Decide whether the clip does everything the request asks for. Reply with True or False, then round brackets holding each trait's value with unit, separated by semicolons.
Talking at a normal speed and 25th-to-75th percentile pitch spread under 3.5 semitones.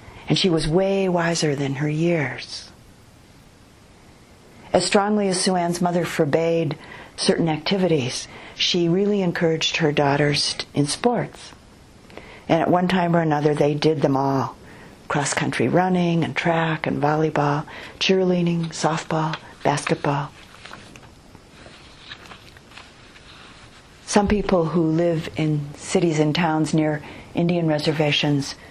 False (115 wpm; 2.7 semitones)